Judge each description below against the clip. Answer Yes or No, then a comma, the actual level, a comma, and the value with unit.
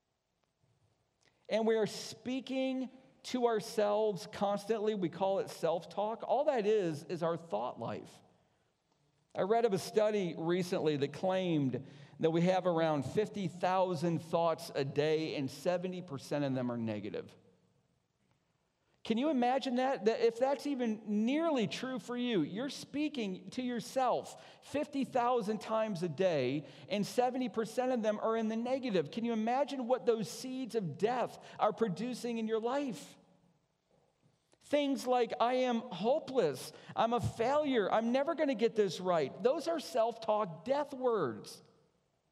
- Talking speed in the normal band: Yes, average, 145 wpm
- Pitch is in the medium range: No, high, 220 Hz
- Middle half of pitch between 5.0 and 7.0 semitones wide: Yes, wide, 5.6 semitones